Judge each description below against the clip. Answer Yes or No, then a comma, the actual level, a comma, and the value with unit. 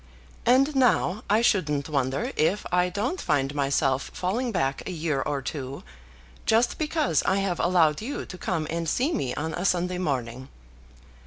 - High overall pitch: No, medium, 175 Hz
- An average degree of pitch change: No, wide, 7.2 semitones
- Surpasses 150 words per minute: Yes, average, 165 wpm